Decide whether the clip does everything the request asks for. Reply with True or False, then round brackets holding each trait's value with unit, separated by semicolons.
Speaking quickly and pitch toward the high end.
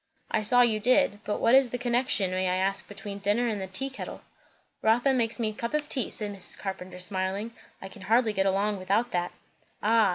True (220 wpm; 210 Hz)